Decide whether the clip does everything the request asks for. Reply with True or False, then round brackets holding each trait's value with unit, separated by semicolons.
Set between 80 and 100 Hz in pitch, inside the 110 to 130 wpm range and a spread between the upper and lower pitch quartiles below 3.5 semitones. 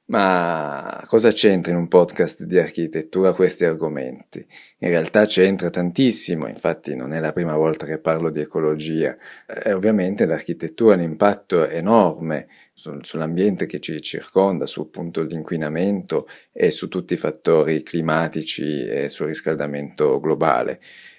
False (85 Hz; 140 wpm; 2.8 semitones)